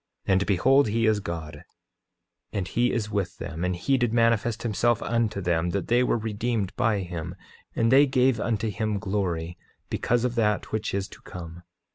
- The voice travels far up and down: No, average, 4.3 semitones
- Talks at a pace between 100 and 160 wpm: No, average, 185 wpm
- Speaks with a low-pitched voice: Yes, low, 105 Hz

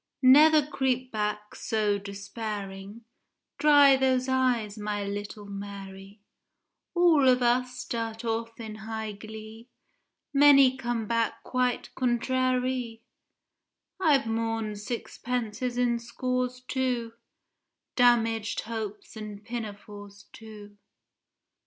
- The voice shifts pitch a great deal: No, average, 3.2 semitones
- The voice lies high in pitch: Yes, high, 230 Hz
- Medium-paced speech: No, slow, 95 wpm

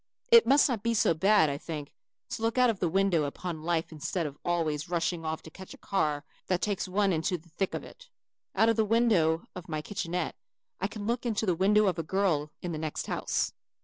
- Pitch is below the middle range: No, medium, 180 Hz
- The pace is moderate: No, fast, 230 wpm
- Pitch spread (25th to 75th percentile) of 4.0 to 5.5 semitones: Yes, average, 4.7 semitones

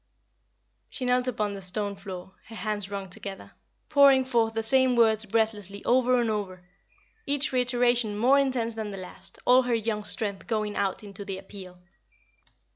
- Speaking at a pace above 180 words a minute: No, average, 165 wpm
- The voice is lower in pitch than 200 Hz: No, high, 220 Hz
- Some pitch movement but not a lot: Yes, average, 3.8 semitones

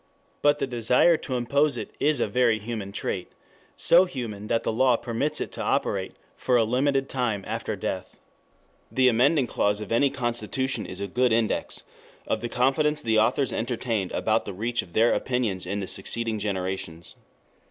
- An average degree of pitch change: Yes, average, 3.5 semitones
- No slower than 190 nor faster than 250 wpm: No, average, 175 wpm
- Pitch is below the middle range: Yes, low, 120 Hz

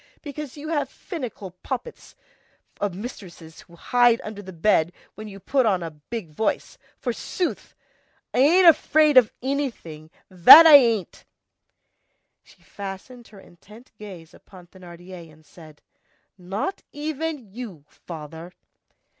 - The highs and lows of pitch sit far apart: Yes, wide, 7.1 semitones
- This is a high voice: Yes, high, 205 Hz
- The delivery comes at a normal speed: No, slow, 130 wpm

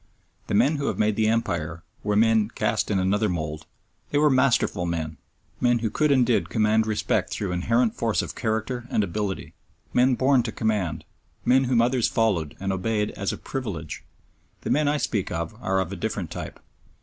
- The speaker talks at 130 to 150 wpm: No, average, 190 wpm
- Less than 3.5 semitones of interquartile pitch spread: No, average, 4.3 semitones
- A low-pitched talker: Yes, low, 110 Hz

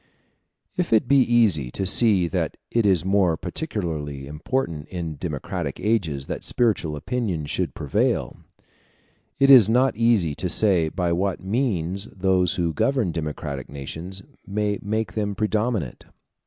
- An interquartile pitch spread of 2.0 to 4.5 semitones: No, wide, 5.6 semitones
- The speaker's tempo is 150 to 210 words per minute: No, average, 140 wpm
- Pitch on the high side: No, very low, 95 Hz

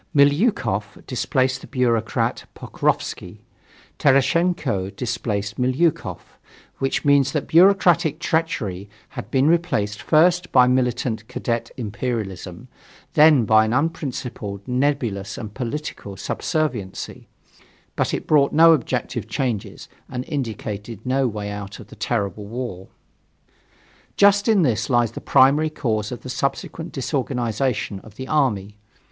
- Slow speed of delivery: Yes, slow, 120 wpm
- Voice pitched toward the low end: Yes, low, 125 Hz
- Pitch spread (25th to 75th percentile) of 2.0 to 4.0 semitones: No, wide, 5.4 semitones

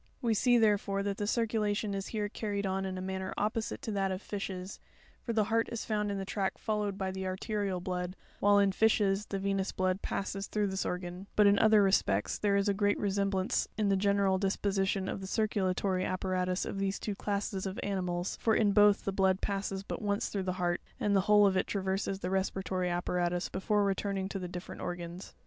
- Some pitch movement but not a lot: No, narrow, 1.5 semitones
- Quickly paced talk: Yes, fast, 215 wpm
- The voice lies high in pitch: Yes, high, 195 Hz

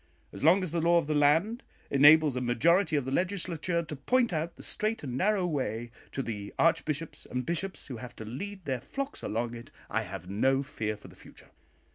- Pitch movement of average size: No, wide, 6.1 semitones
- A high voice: No, medium, 150 Hz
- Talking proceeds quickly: Yes, fast, 210 wpm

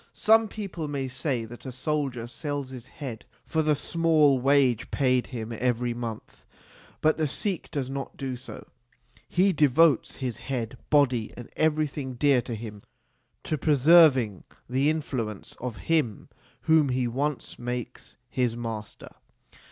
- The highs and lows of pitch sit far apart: No, average, 3.8 semitones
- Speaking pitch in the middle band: No, low, 130 Hz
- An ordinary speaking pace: Yes, average, 145 wpm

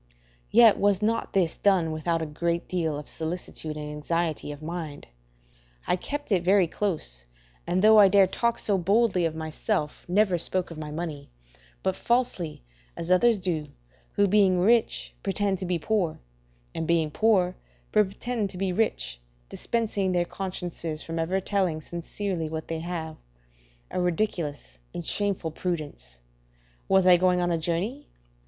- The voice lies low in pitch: No, medium, 180 Hz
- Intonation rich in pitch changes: No, average, 3.7 semitones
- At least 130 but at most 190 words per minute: Yes, average, 155 wpm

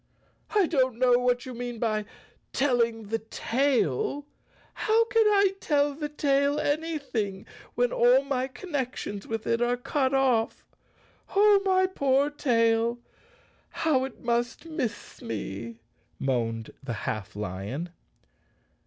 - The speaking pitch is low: No, very high, 250 Hz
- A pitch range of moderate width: Yes, average, 4.4 semitones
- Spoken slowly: Yes, slow, 125 wpm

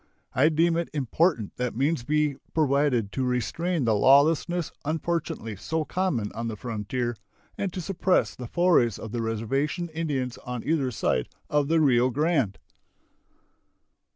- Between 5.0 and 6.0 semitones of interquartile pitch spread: Yes, wide, 5.4 semitones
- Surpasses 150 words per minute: No, average, 145 wpm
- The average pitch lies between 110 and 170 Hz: Yes, medium, 140 Hz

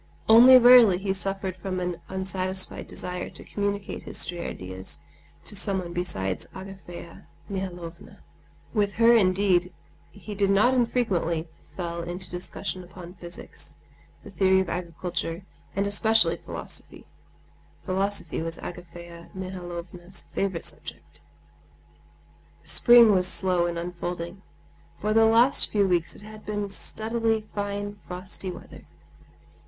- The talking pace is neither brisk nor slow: No, slow, 120 wpm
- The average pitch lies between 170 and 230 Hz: Yes, high, 190 Hz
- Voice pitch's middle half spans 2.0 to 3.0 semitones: Yes, narrow, 2.6 semitones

